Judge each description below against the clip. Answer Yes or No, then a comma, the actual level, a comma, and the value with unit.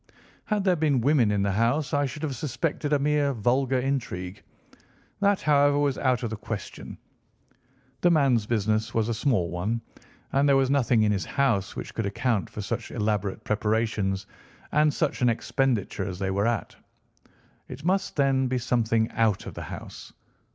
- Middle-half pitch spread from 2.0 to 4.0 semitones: No, average, 4.8 semitones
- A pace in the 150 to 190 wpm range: Yes, average, 175 wpm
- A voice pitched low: Yes, low, 120 Hz